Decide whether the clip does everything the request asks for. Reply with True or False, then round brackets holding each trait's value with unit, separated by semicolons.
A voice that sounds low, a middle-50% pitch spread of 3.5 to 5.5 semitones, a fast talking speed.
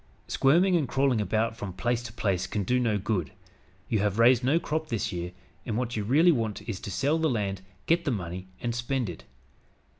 True (115 Hz; 4.7 semitones; 210 wpm)